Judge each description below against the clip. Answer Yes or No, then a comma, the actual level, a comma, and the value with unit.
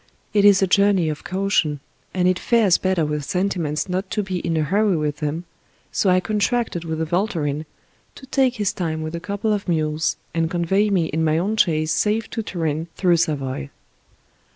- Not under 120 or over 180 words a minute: No, average, 200 wpm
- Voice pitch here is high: No, medium, 180 Hz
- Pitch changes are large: No, average, 4.1 semitones